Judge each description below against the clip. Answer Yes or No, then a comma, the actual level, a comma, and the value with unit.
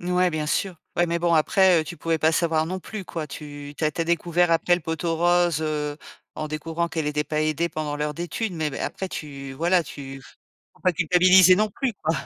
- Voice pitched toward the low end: No, medium, 165 Hz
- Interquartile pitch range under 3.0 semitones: Yes, narrow, 2.5 semitones